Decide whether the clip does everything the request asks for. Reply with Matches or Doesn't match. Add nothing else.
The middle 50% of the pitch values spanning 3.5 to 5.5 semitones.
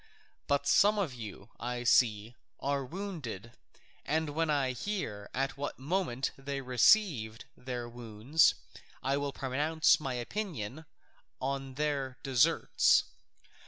Matches